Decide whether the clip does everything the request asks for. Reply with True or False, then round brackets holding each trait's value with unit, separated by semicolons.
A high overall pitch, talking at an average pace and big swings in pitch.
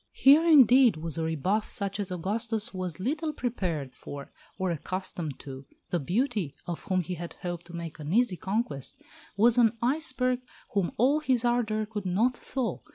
True (200 Hz; 170 wpm; 6.0 semitones)